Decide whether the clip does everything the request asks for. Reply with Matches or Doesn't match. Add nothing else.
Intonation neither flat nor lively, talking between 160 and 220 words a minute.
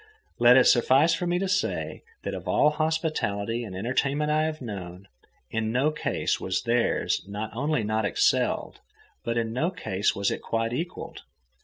Doesn't match